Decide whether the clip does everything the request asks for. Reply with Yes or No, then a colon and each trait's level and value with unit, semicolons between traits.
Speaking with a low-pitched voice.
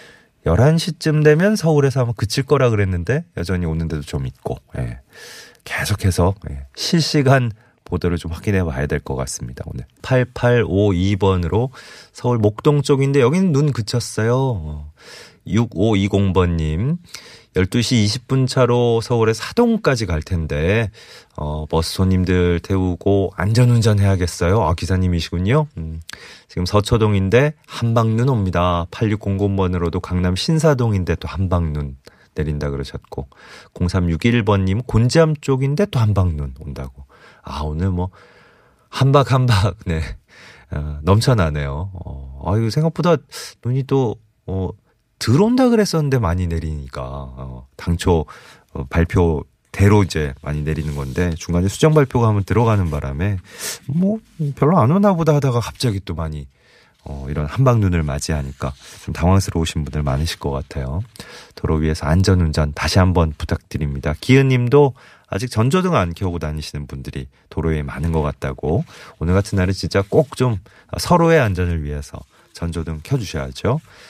Yes: very low, 95 Hz